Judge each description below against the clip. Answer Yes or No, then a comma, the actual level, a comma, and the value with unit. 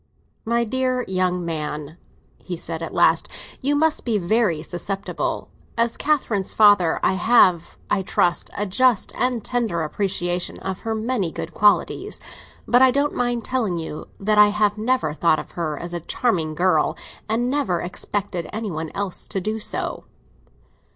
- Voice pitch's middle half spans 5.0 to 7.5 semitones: Yes, average, 5.3 semitones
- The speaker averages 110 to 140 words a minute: No, average, 160 wpm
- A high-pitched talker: Yes, high, 205 Hz